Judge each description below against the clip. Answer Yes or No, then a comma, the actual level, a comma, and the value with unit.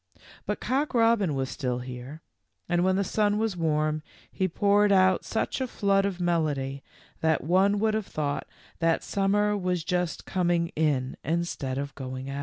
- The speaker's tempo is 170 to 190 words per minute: Yes, average, 175 wpm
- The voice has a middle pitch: Yes, medium, 175 Hz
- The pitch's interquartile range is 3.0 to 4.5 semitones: No, average, 5.3 semitones